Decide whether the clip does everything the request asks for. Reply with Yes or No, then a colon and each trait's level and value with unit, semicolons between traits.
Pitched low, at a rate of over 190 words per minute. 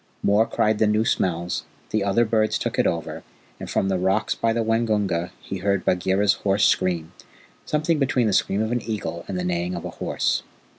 Yes: low, 100 Hz; average, 200 wpm